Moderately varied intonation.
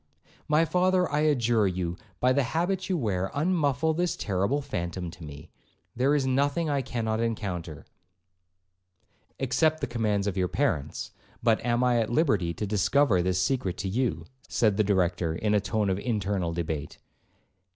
No: wide, 7.2 semitones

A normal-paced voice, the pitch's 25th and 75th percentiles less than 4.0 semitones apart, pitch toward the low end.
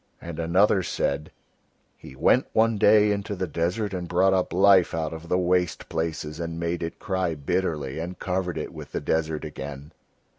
Yes: average, 180 wpm; average, 2.8 semitones; very low, 85 Hz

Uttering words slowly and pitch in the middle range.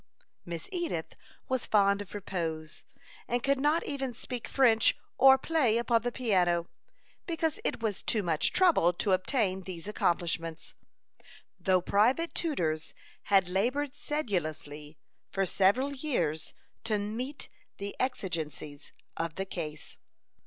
No: slow, 125 wpm; high, 205 Hz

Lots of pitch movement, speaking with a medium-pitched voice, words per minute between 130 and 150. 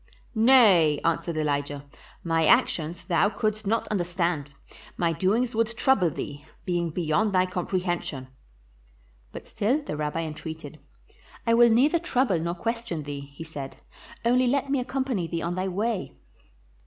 Yes: wide, 6.2 semitones; medium, 180 Hz; average, 140 wpm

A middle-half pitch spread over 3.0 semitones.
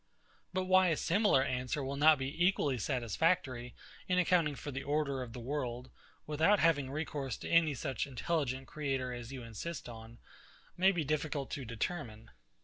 Yes: average, 4.4 semitones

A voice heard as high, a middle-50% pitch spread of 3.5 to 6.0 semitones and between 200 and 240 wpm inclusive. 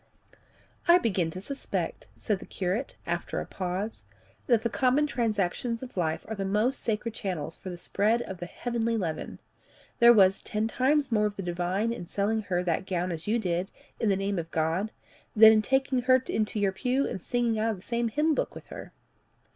Yes: high, 210 Hz; average, 4.3 semitones; fast, 205 wpm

